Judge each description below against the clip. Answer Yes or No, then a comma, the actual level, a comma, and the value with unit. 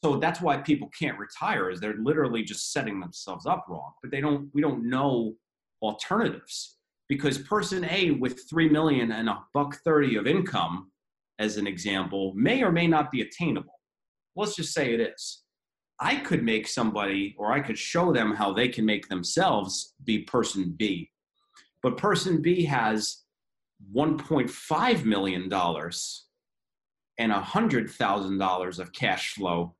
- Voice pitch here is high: No, low, 120 Hz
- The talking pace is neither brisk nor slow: Yes, average, 155 wpm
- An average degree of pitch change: No, wide, 7.2 semitones